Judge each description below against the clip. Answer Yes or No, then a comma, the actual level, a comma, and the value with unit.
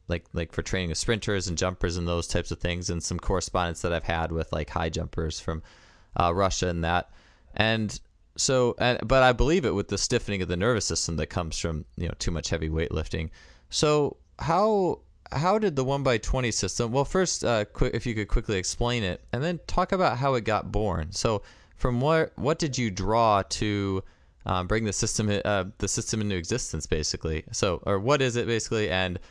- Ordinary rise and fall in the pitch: No, wide, 5.7 semitones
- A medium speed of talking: No, fast, 215 wpm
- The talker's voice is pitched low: Yes, low, 100 Hz